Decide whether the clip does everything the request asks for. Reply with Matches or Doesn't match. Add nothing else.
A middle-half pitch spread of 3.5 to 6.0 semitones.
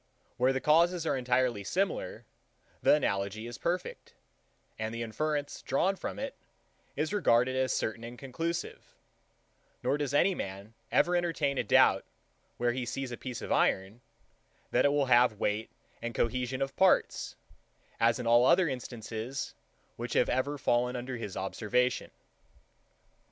Matches